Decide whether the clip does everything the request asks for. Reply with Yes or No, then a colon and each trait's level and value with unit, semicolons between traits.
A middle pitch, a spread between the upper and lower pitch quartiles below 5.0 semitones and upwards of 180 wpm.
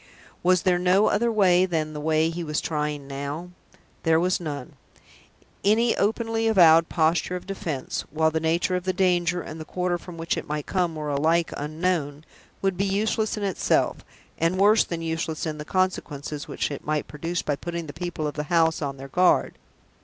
Yes: medium, 165 Hz; average, 3.1 semitones; average, 190 wpm